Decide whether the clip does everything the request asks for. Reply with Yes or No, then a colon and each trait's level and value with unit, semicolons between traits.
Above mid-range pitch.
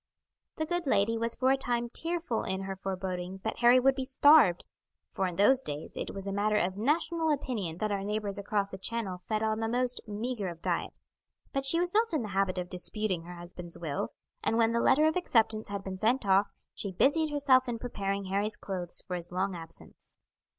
Yes: high, 215 Hz